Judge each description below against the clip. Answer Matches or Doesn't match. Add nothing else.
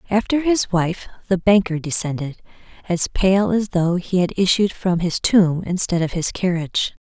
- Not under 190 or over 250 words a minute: Doesn't match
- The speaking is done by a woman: Matches